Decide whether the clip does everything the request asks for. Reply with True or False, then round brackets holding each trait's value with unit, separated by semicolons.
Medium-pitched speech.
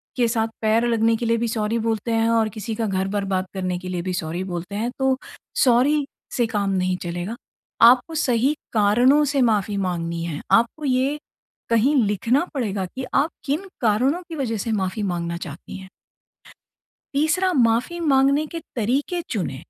False (225 Hz)